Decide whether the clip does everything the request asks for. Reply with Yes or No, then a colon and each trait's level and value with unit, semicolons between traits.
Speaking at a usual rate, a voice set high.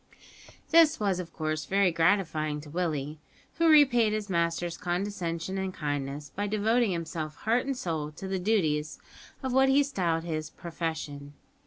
No: average, 155 wpm; medium, 175 Hz